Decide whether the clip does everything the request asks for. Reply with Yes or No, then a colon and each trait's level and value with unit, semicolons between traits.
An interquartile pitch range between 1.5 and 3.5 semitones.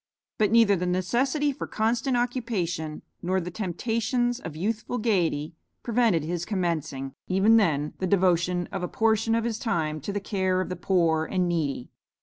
No: average, 4.8 semitones